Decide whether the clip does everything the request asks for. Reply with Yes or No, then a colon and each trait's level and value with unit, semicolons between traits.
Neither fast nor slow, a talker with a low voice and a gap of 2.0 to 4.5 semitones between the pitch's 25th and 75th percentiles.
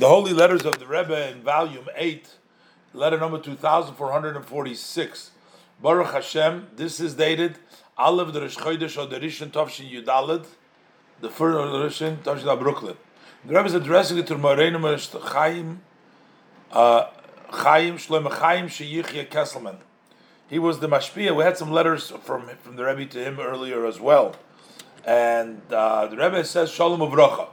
No: average, 155 wpm; medium, 155 Hz; average, 3.1 semitones